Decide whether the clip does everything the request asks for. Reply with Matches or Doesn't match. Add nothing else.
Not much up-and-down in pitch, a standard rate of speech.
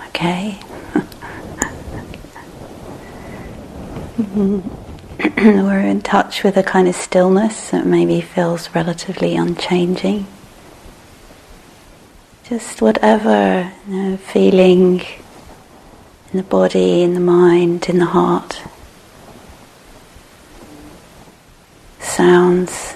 Doesn't match